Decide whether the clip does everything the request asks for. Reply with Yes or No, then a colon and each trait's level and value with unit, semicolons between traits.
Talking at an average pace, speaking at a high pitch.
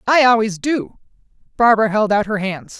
Yes: average, 170 wpm; high, 215 Hz